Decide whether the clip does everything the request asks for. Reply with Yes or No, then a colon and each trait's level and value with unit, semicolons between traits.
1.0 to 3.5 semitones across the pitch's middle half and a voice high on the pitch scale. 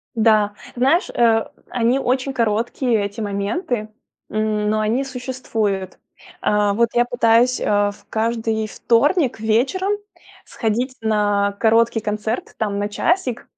Yes: average, 2.7 semitones; high, 225 Hz